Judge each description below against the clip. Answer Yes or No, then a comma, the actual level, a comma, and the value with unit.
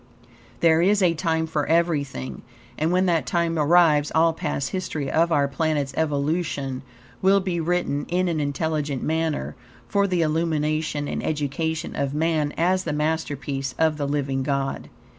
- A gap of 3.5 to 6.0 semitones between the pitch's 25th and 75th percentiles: No, average, 2.7 semitones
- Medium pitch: Yes, medium, 160 Hz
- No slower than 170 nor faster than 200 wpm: No, average, 155 wpm